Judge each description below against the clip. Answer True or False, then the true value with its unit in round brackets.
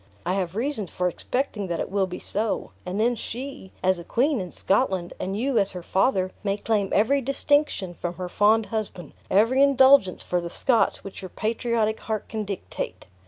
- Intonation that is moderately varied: True (4.3 semitones)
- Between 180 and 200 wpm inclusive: True (190 wpm)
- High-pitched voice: True (205 Hz)